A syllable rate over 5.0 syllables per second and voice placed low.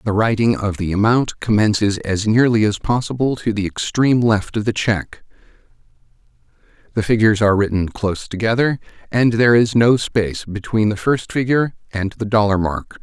Yes: 5.5 syllables/s; low, 110 Hz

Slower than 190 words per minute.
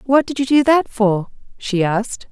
No: fast, 205 wpm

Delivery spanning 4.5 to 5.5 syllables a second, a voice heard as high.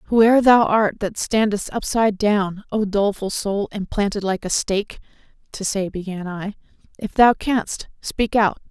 Yes: 4.7 syllables/s; high, 205 Hz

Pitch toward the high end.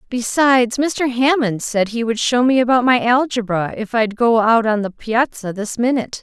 Yes: high, 235 Hz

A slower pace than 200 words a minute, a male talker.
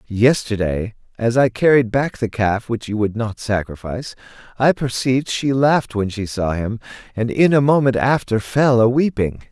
Yes: average, 175 wpm; male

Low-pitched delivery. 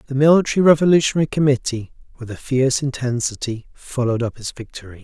Yes: low, 130 Hz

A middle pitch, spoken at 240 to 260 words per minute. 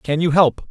Yes: medium, 155 Hz; fast, 255 wpm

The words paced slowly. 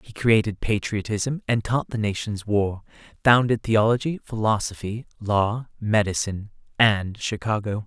Yes: slow, 105 wpm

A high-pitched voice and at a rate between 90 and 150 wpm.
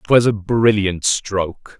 No: low, 105 Hz; slow, 135 wpm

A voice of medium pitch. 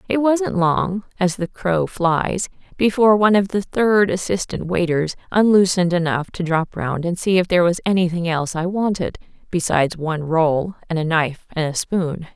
Yes: medium, 180 Hz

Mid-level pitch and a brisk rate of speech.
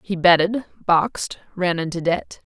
No: medium, 180 Hz; average, 140 wpm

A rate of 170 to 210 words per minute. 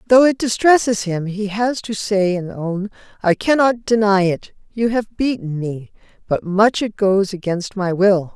Yes: average, 180 wpm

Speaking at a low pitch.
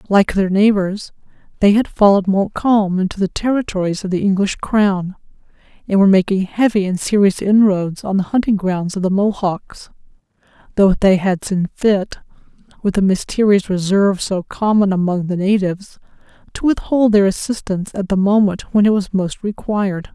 No: high, 195 Hz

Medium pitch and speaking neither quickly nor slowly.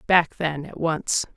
Yes: medium, 160 Hz; average, 175 wpm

